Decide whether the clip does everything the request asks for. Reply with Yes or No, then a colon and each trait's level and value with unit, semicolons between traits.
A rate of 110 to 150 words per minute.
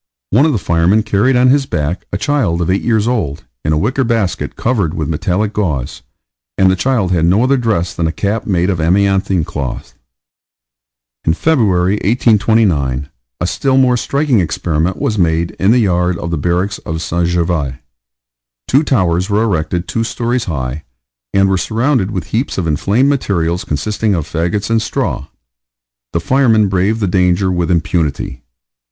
No: average, 170 wpm